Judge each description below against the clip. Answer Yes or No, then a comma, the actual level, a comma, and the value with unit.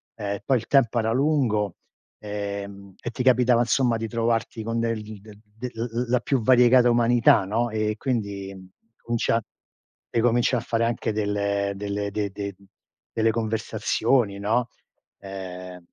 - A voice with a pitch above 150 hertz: No, low, 110 Hz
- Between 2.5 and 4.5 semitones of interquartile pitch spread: Yes, average, 2.8 semitones